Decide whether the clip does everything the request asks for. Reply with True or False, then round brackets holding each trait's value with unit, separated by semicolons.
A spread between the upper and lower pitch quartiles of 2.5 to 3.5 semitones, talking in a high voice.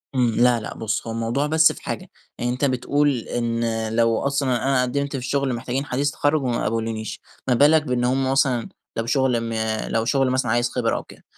False (3.0 semitones; 125 Hz)